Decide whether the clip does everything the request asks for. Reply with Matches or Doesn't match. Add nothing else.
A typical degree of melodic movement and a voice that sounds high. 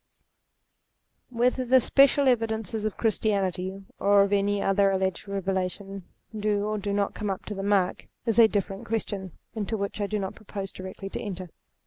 Doesn't match